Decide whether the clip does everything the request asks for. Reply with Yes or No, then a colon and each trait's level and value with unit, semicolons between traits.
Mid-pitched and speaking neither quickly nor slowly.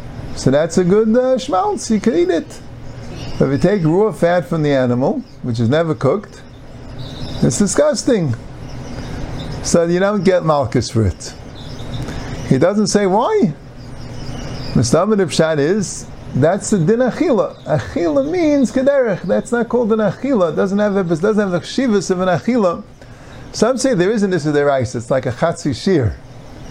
Yes: medium, 160 Hz; average, 170 wpm